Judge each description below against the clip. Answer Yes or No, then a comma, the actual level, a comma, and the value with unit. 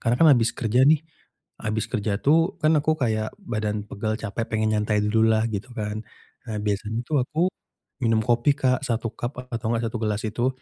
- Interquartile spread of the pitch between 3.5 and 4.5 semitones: No, average, 3.0 semitones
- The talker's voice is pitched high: No, low, 115 Hz